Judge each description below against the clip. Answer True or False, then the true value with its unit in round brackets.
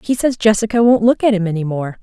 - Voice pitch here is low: False (210 Hz)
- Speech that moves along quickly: True (265 wpm)